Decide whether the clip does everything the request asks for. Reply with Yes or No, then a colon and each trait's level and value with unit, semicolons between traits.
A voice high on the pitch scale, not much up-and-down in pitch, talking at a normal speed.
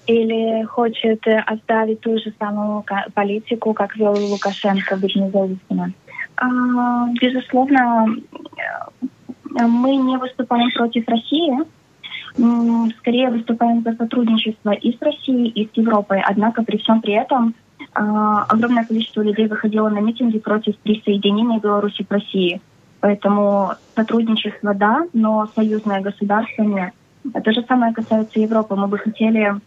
Yes: high, 220 Hz; narrow, 2.3 semitones; average, 120 wpm